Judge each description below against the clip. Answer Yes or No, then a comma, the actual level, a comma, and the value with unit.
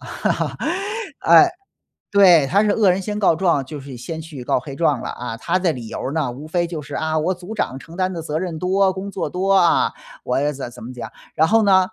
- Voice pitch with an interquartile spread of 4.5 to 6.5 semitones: Yes, average, 5.0 semitones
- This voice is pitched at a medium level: Yes, medium, 165 Hz